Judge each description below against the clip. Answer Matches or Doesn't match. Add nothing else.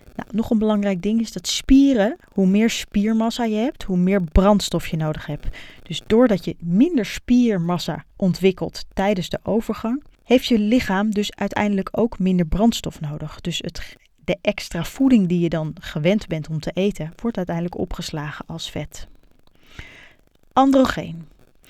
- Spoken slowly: Doesn't match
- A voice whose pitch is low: Doesn't match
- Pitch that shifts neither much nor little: Matches